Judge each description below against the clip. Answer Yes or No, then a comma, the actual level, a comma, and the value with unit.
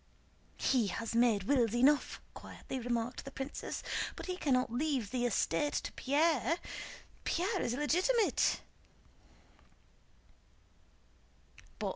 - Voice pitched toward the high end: Yes, very high, 260 Hz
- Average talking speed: No, slow, 100 wpm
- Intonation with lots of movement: No, average, 4.0 semitones